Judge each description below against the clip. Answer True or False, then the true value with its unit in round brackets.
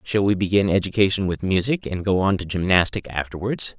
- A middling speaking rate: True (190 wpm)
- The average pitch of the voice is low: True (95 Hz)